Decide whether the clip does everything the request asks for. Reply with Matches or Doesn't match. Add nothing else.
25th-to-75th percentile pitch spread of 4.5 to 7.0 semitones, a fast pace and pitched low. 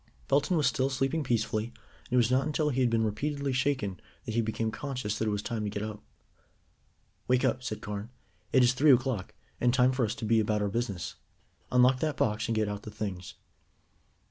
Doesn't match